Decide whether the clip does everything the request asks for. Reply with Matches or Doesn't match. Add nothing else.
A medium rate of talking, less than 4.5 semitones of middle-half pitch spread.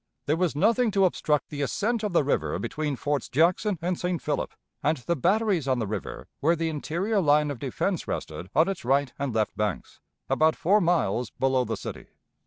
Doesn't match